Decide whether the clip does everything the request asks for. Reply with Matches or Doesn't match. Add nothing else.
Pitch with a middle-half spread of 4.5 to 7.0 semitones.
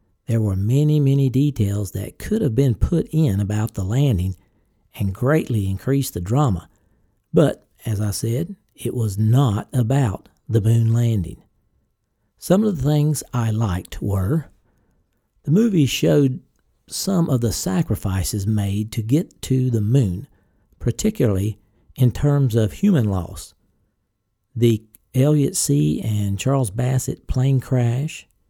Matches